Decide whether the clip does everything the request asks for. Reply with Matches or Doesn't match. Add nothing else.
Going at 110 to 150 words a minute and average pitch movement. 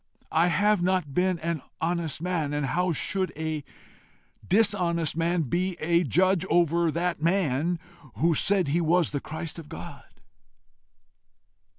Doesn't match